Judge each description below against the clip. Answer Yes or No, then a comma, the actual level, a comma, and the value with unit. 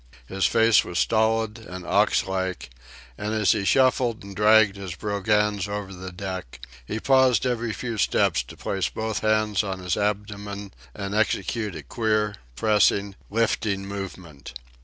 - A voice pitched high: No, low, 105 Hz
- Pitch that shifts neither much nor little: No, narrow, 2.1 semitones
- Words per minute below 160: Yes, average, 150 wpm